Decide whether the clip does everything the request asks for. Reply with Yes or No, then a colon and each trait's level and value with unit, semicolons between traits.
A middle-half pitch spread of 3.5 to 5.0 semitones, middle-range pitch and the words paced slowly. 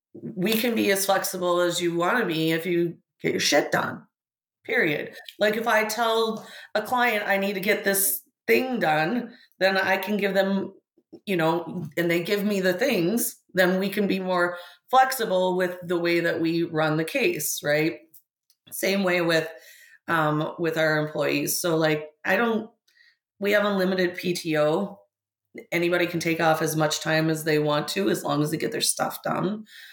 No: average, 3.8 semitones; medium, 180 Hz; average, 185 wpm